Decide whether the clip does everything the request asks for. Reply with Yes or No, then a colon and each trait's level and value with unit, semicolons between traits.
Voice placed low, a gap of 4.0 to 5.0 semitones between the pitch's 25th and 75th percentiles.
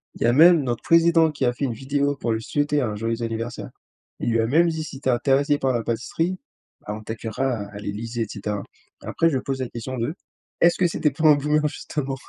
Yes: low, 130 Hz; average, 4.5 semitones